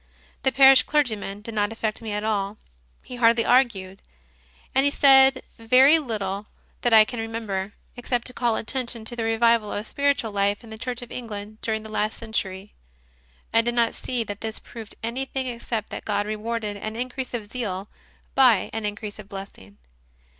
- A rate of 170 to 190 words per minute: Yes, average, 180 wpm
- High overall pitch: Yes, high, 225 Hz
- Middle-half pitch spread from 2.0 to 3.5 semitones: Yes, average, 2.8 semitones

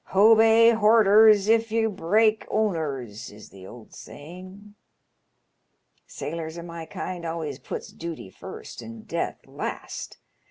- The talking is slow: Yes, slow, 125 wpm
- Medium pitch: Yes, medium, 180 Hz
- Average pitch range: No, wide, 6.3 semitones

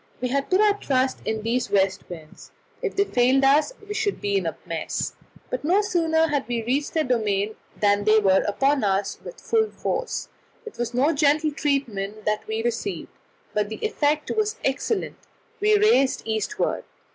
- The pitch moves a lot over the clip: Yes, wide, 7.3 semitones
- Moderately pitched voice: No, very high, 265 Hz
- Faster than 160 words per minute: Yes, average, 185 wpm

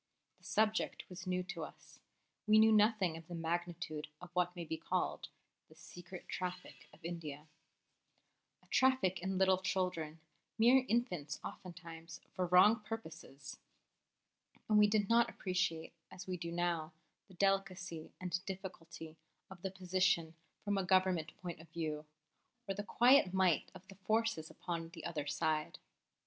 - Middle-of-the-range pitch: Yes, medium, 180 Hz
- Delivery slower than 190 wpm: Yes, average, 150 wpm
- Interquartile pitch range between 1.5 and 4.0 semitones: Yes, average, 2.9 semitones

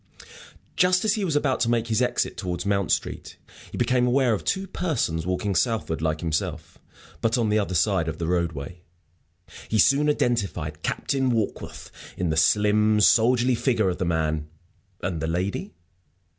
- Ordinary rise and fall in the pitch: No, wide, 6.2 semitones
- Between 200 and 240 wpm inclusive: No, average, 170 wpm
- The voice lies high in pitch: No, low, 105 Hz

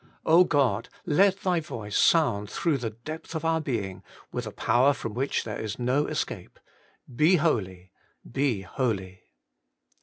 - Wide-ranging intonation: Yes, wide, 6.9 semitones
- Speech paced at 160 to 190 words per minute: No, average, 145 wpm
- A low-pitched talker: Yes, low, 125 Hz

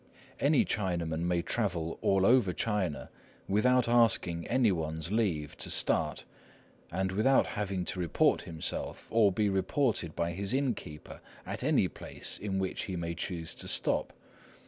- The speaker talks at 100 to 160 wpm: Yes, average, 145 wpm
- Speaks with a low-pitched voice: Yes, very low, 95 Hz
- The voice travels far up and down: No, average, 4.7 semitones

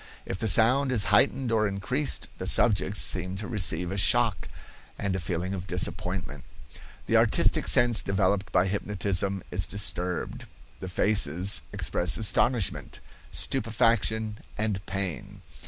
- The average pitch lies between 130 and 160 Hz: No, low, 100 Hz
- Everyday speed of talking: No, slow, 130 wpm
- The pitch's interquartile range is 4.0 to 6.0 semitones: No, average, 3.1 semitones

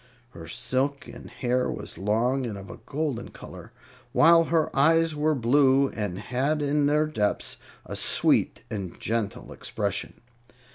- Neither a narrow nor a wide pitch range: Yes, average, 5.0 semitones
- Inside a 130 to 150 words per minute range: Yes, average, 140 wpm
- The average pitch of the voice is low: Yes, low, 130 Hz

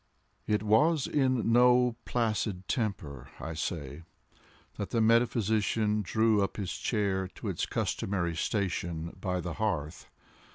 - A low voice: Yes, low, 105 Hz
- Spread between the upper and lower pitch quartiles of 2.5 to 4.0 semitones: No, average, 4.6 semitones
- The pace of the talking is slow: Yes, slow, 125 wpm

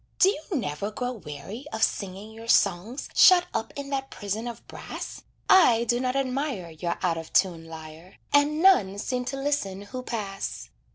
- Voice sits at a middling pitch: No, high, 225 Hz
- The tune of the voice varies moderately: No, wide, 6.3 semitones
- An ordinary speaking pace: Yes, average, 175 wpm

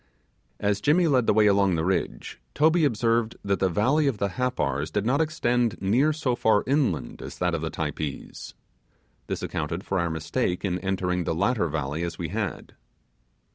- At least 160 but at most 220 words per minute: Yes, average, 180 wpm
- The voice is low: Yes, low, 100 Hz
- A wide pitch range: Yes, wide, 6.4 semitones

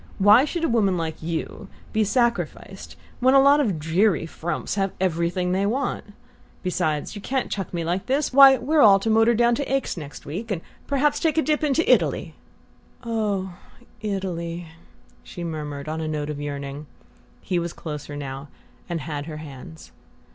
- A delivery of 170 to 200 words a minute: Yes, average, 180 wpm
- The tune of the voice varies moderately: No, wide, 6.8 semitones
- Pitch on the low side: No, medium, 185 Hz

